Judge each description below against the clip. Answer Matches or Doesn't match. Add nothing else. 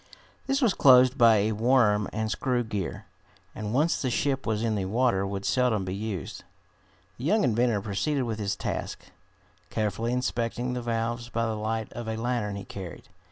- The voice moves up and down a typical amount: Matches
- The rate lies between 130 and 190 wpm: Matches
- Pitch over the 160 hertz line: Doesn't match